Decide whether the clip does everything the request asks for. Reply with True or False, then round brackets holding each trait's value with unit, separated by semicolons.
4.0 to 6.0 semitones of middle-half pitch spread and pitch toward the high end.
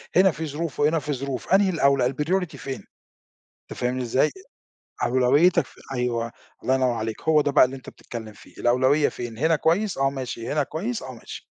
False (4.4 semitones; 135 Hz)